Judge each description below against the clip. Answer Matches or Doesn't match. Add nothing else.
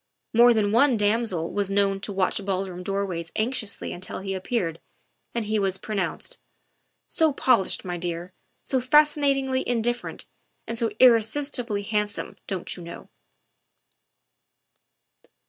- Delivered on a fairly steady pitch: Doesn't match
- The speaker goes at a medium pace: Doesn't match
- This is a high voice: Matches